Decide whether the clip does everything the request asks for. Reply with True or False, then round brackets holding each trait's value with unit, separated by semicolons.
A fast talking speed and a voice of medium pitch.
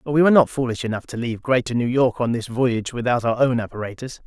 False (255 wpm; 120 Hz)